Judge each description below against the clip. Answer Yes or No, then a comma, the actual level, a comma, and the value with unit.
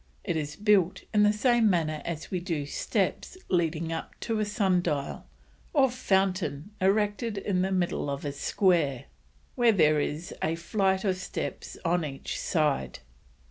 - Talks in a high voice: No, medium, 180 Hz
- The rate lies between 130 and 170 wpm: Yes, average, 160 wpm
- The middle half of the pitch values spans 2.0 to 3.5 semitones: No, average, 4.8 semitones